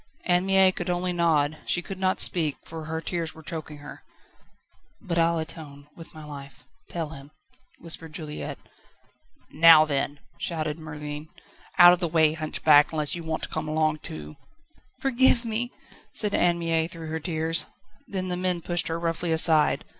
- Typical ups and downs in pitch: No, narrow, 2.3 semitones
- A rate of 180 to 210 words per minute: No, average, 170 wpm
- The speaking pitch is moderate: Yes, medium, 160 Hz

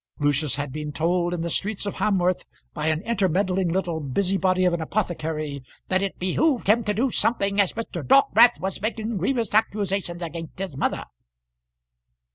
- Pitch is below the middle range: No, medium, 185 Hz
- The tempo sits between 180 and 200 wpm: No, average, 165 wpm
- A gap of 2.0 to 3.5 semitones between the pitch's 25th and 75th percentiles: No, average, 4.1 semitones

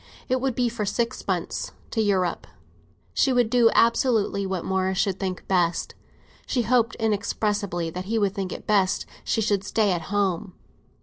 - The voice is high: Yes, high, 205 Hz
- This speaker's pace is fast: No, average, 170 wpm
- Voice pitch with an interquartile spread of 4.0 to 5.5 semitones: No, average, 3.4 semitones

